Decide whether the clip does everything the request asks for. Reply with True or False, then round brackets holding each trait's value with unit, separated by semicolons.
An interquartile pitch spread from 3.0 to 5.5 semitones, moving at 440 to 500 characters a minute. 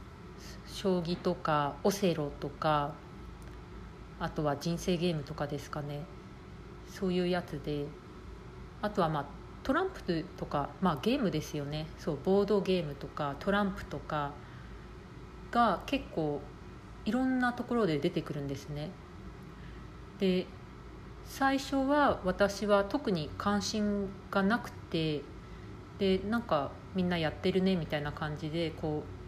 False (5.1 semitones; 245 characters per minute)